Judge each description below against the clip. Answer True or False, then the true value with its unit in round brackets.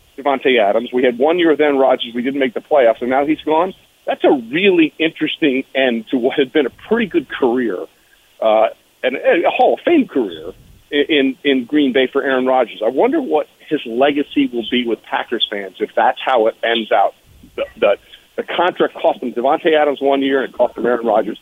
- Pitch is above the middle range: False (140 Hz)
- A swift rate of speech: True (215 wpm)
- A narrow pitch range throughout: False (3.4 semitones)